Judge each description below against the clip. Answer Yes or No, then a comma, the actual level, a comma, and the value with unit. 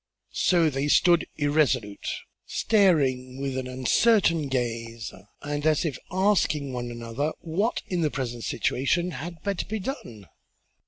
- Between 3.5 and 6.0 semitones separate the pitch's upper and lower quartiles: Yes, average, 5.3 semitones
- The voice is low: No, medium, 145 Hz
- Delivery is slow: Yes, slow, 130 wpm